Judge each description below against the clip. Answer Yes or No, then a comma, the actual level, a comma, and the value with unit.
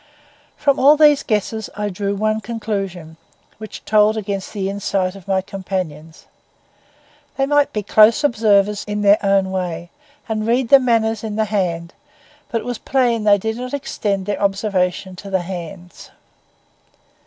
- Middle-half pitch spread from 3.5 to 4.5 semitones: No, average, 2.7 semitones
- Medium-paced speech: Yes, average, 160 wpm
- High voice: Yes, high, 205 Hz